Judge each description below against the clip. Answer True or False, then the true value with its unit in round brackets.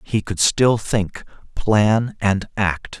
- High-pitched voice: False (105 Hz)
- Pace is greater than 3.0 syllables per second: False (2.8 syllables/s)